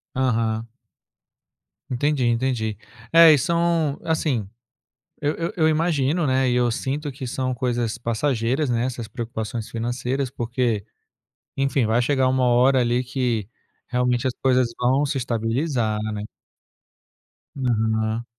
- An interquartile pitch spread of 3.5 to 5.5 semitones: No, average, 2.8 semitones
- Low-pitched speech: Yes, low, 125 Hz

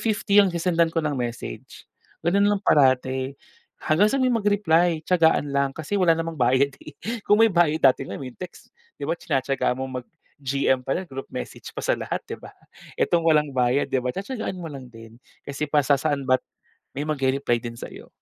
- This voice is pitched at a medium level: Yes, medium, 150 Hz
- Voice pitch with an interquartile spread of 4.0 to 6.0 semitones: Yes, average, 4.7 semitones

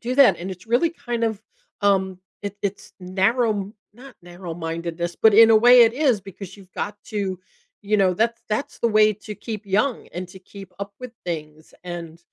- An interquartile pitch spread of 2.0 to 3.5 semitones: No, average, 3.9 semitones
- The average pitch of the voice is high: Yes, high, 200 Hz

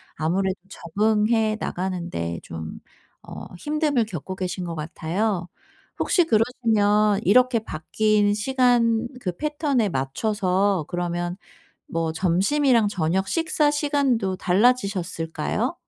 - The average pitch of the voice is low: No, high, 205 Hz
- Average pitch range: Yes, average, 5.0 semitones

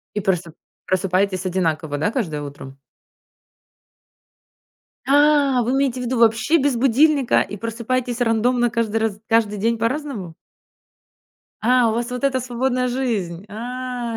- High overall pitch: Yes, high, 230 Hz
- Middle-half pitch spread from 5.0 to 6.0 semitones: No, average, 4.1 semitones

